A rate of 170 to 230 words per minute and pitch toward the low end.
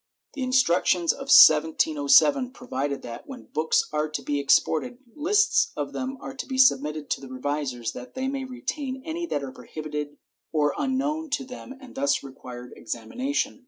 No: average, 175 wpm; medium, 175 Hz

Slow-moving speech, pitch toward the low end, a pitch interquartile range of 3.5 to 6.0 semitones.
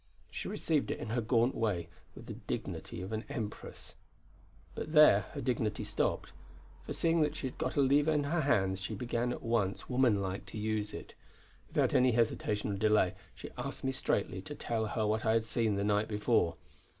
No: average, 200 wpm; low, 110 Hz; average, 3.8 semitones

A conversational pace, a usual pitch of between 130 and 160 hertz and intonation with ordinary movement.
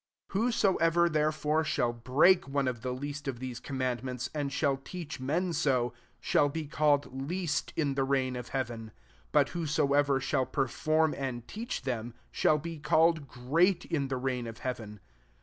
Yes: average, 175 wpm; medium, 140 Hz; average, 3.5 semitones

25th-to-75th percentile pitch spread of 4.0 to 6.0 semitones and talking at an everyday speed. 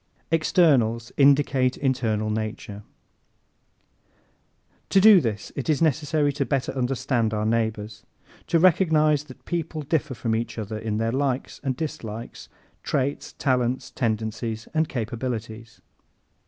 No: average, 4.8 semitones; slow, 125 wpm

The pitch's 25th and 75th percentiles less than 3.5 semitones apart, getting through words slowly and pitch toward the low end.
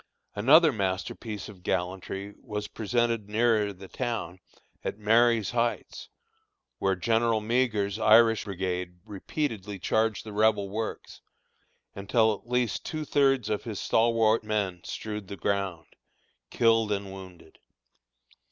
Yes: average, 2.8 semitones; slow, 120 wpm; low, 105 Hz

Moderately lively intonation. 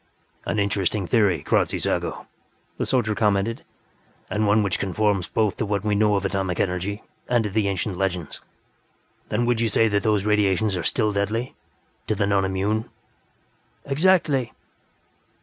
No: narrow, 2.1 semitones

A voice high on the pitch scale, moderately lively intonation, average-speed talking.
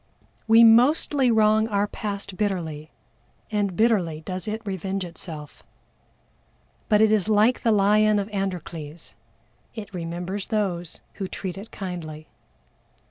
No: high, 200 Hz; average, 3.5 semitones; slow, 125 wpm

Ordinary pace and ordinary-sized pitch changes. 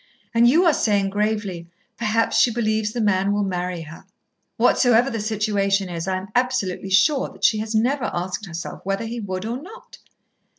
Yes: average, 180 wpm; average, 3.5 semitones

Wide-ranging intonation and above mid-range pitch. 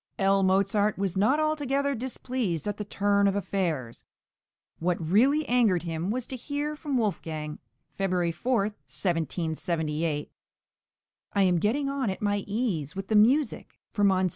Yes: wide, 6.0 semitones; high, 200 Hz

